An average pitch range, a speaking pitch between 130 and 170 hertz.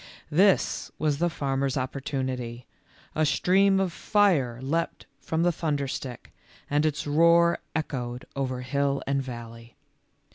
Yes: average, 4.4 semitones; medium, 140 Hz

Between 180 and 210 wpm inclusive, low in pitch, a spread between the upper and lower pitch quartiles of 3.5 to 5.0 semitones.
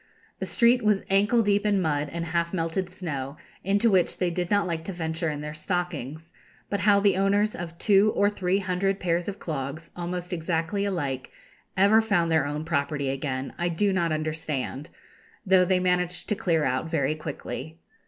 No: average, 185 wpm; medium, 175 Hz; average, 3.8 semitones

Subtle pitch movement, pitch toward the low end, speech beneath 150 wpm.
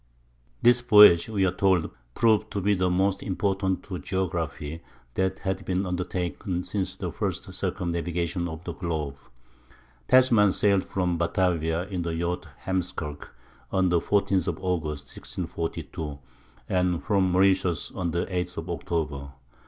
Yes: narrow, 2.1 semitones; very low, 90 Hz; average, 140 wpm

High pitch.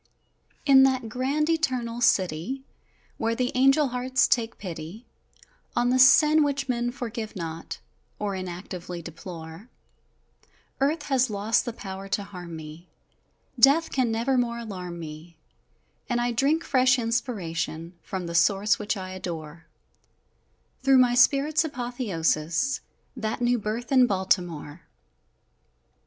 Yes: high, 230 Hz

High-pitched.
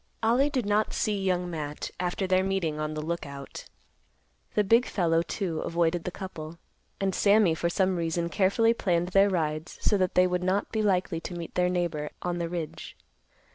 No: medium, 180 Hz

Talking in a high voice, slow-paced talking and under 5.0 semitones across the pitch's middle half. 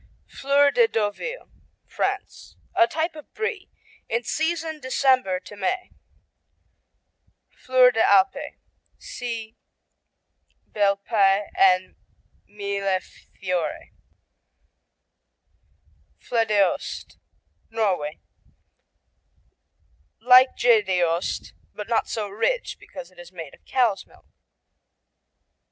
No: high, 220 Hz; slow, 80 wpm; average, 5.3 semitones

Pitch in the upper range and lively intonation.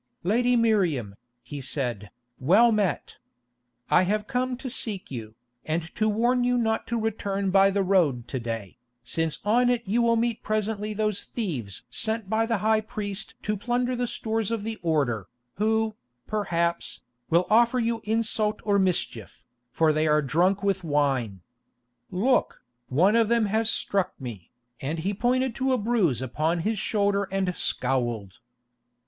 Yes: high, 200 Hz; wide, 6.2 semitones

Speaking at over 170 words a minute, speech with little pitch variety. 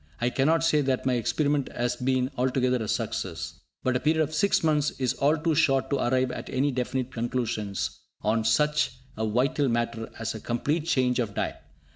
No: average, 190 wpm; average, 3.6 semitones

